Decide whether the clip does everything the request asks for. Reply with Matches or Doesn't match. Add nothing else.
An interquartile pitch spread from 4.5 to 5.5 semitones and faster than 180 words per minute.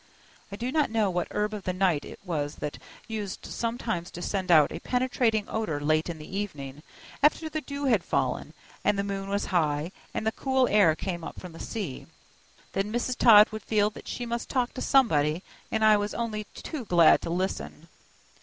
Matches